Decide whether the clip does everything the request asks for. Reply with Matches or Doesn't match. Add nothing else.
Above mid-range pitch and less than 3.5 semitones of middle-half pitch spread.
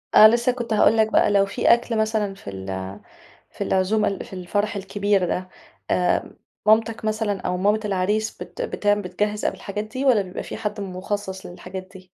Matches